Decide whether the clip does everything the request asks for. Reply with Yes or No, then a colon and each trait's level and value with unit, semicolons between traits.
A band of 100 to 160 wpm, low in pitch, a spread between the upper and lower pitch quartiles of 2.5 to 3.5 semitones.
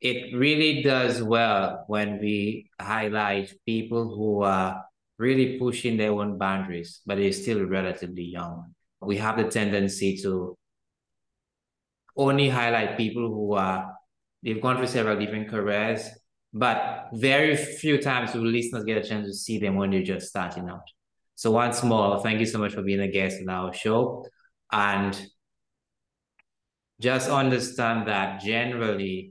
Yes: average, 145 wpm; low, 105 Hz; average, 3.2 semitones